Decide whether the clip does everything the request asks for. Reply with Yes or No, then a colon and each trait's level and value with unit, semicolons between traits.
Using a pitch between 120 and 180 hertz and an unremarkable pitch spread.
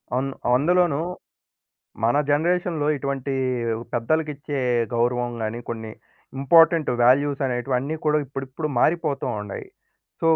Yes: medium, 140 Hz; average, 3.8 semitones